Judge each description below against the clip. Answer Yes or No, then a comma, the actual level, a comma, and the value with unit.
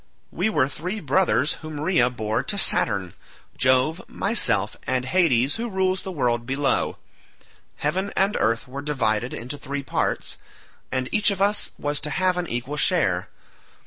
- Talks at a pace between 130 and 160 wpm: Yes, average, 150 wpm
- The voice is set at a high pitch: No, medium, 145 Hz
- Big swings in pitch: Yes, wide, 6.6 semitones